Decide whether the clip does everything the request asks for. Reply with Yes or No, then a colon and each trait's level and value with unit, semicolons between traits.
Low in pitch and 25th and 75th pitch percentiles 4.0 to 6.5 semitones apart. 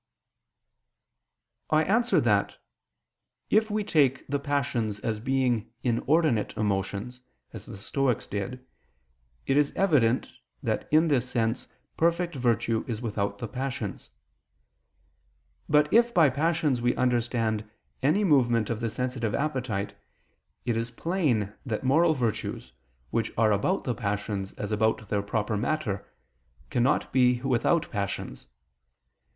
Yes: low, 125 Hz; average, 5.0 semitones